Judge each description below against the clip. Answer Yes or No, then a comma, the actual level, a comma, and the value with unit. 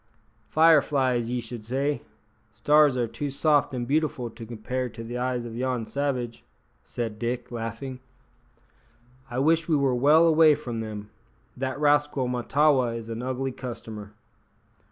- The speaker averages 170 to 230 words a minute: No, average, 150 wpm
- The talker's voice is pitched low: Yes, low, 125 Hz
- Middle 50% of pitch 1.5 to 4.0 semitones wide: Yes, average, 3.5 semitones